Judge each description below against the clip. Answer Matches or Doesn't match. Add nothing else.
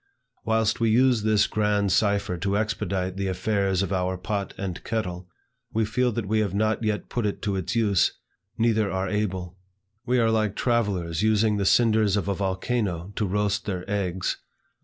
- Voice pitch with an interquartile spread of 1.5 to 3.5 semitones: Matches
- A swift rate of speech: Doesn't match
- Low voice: Matches